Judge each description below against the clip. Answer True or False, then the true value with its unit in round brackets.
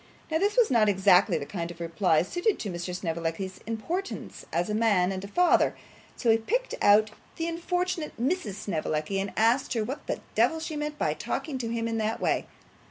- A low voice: False (220 Hz)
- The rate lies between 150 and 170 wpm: False (200 wpm)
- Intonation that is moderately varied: False (8.5 semitones)